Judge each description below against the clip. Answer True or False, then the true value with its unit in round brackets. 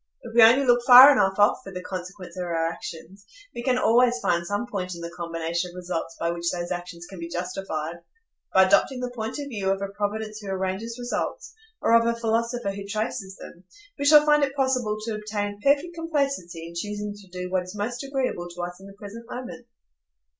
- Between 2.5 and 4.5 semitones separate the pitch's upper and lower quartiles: False (5.0 semitones)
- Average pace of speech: False (215 wpm)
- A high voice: True (205 Hz)